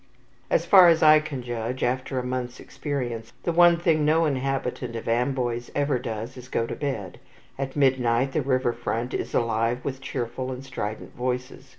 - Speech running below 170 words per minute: No, average, 185 wpm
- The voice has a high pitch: No, low, 130 Hz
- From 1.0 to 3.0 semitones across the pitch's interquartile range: Yes, average, 2.7 semitones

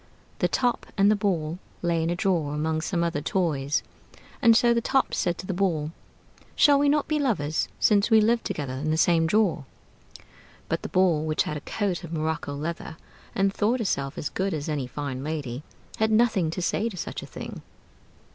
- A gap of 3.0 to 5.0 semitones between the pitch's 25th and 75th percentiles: No, wide, 5.4 semitones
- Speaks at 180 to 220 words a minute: Yes, average, 200 wpm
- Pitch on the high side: No, medium, 170 Hz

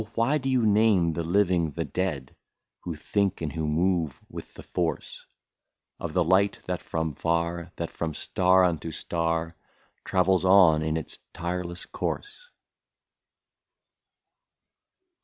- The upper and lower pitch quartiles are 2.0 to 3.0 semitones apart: Yes, narrow, 2.5 semitones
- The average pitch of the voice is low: Yes, very low, 85 Hz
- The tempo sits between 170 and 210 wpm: No, slow, 135 wpm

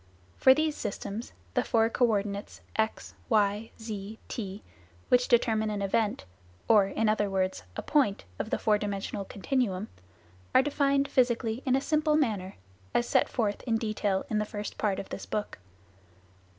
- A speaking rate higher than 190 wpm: No, average, 165 wpm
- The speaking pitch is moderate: No, high, 215 Hz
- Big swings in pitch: No, average, 3.0 semitones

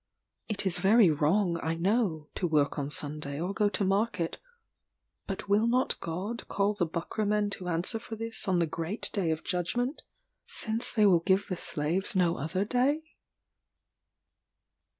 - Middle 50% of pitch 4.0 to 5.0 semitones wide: Yes, average, 4.3 semitones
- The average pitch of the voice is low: No, high, 190 Hz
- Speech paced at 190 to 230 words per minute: No, average, 165 wpm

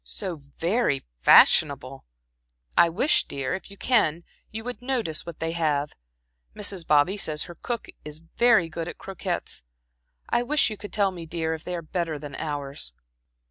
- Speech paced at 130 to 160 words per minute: No, average, 170 wpm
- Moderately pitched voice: Yes, medium, 170 Hz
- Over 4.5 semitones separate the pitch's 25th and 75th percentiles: Yes, average, 5.1 semitones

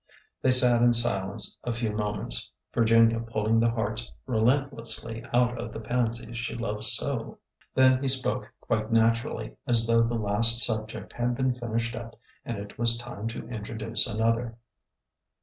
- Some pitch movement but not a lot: No, narrow, 1.3 semitones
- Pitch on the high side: No, low, 115 Hz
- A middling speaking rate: Yes, average, 180 wpm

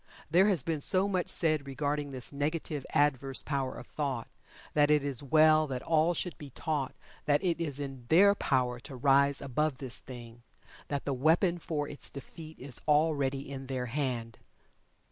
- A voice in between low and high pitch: Yes, medium, 145 Hz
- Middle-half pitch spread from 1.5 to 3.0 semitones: Yes, average, 2.7 semitones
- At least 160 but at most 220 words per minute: Yes, average, 175 wpm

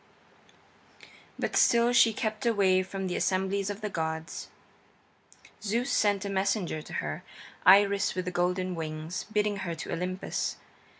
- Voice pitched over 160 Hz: Yes, high, 190 Hz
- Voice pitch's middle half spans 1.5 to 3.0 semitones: Yes, narrow, 2.4 semitones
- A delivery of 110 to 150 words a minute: Yes, average, 145 wpm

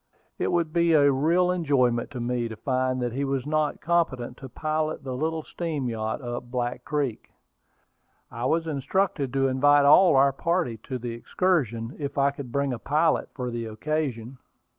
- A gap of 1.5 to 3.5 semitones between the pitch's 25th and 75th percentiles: No, average, 4.0 semitones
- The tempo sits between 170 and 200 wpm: Yes, average, 180 wpm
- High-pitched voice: No, medium, 140 Hz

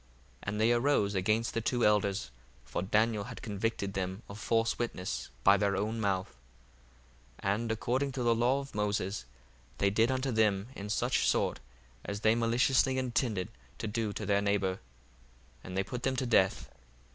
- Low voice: Yes, low, 110 Hz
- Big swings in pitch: No, average, 3.0 semitones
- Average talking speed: Yes, average, 175 wpm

